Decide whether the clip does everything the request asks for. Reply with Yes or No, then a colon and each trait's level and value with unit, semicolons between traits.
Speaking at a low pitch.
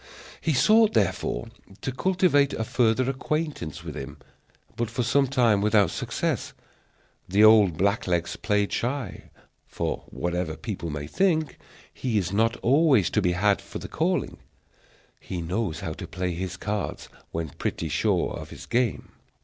Yes: low, 105 Hz